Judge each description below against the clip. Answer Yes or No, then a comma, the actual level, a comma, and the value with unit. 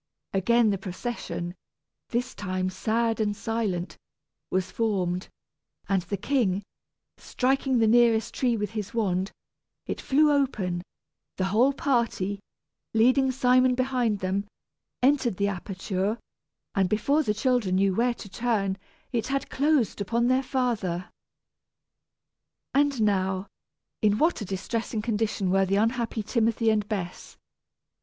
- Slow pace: Yes, slow, 130 wpm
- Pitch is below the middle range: No, high, 220 Hz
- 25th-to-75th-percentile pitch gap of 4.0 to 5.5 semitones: Yes, average, 4.3 semitones